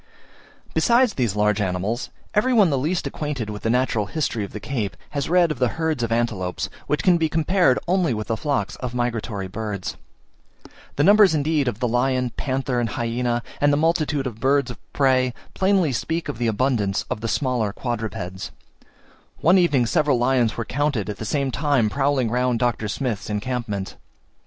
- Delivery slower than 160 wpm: No, average, 180 wpm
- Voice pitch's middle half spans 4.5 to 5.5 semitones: Yes, average, 4.8 semitones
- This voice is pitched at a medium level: No, low, 125 Hz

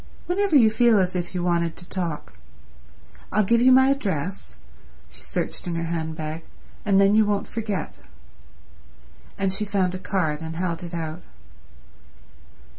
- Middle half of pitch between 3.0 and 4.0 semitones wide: No, average, 4.4 semitones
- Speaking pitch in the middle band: Yes, medium, 180 Hz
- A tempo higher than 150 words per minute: No, average, 145 wpm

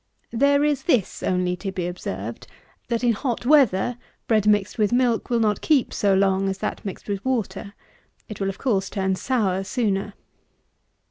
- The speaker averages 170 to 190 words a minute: Yes, average, 175 wpm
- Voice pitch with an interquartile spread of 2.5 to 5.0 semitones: Yes, average, 4.1 semitones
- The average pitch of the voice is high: Yes, high, 210 Hz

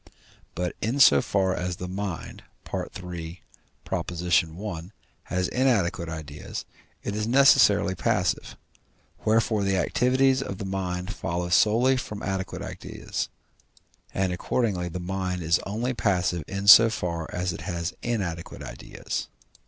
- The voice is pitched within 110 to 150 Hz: No, very low, 95 Hz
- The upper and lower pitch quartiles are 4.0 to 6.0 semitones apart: No, average, 3.4 semitones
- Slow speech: Yes, slow, 130 wpm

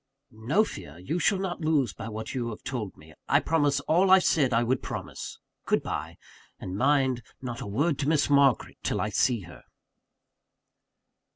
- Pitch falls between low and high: No, low, 130 Hz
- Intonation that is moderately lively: No, wide, 5.7 semitones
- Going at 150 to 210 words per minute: Yes, average, 180 wpm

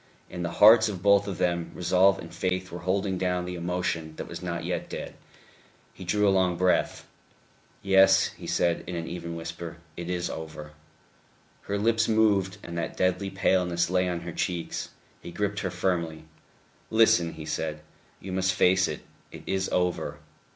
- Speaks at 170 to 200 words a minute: Yes, average, 175 wpm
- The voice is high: No, very low, 90 Hz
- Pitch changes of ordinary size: No, narrow, 2.0 semitones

